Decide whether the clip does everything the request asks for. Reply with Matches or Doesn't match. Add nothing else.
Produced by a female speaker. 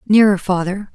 Matches